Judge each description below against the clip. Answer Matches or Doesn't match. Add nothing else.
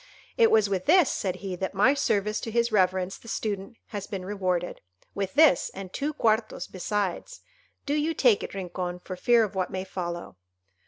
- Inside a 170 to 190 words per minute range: Matches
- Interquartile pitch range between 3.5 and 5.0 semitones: Matches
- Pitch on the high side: Matches